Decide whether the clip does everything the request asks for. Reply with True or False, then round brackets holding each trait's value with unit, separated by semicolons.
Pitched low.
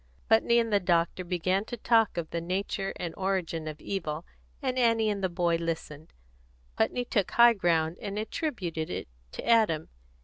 False (185 Hz)